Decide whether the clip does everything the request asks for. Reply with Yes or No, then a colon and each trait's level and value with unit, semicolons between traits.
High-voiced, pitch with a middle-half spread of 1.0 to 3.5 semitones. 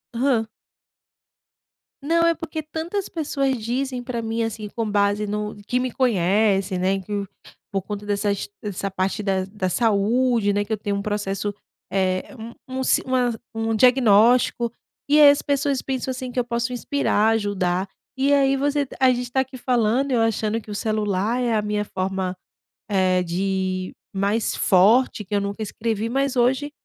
No: high, 220 Hz; average, 4.2 semitones